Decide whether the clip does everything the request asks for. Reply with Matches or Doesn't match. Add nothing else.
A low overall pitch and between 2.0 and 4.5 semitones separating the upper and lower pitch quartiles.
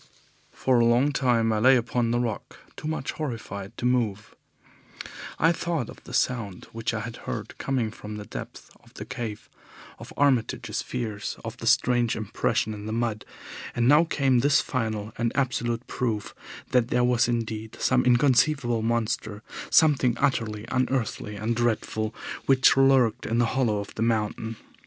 Matches